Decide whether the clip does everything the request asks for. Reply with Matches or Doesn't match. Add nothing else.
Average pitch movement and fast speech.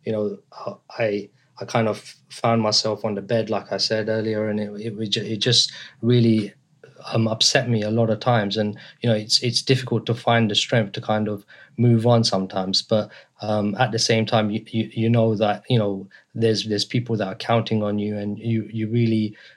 Doesn't match